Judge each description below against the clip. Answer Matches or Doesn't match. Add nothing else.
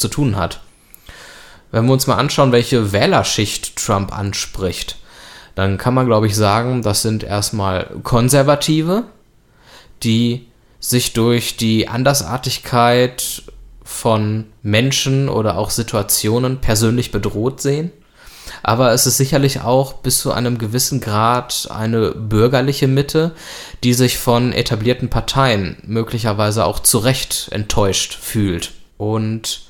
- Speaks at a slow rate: Matches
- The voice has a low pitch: Matches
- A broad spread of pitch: Doesn't match